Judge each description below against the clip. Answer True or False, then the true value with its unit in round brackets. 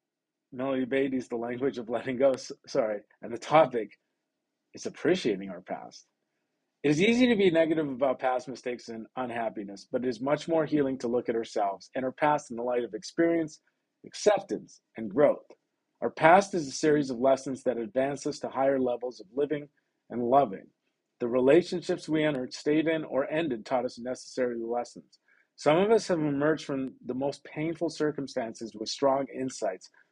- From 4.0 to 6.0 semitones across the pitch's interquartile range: False (3.6 semitones)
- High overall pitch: False (135 Hz)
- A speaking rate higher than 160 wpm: True (175 wpm)